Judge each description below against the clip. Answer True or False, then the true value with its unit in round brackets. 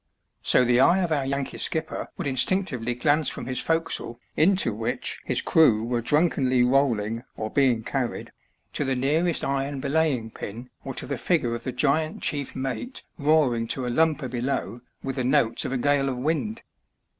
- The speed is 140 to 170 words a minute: False (180 wpm)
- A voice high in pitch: False (135 Hz)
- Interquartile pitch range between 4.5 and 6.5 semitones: False (3.8 semitones)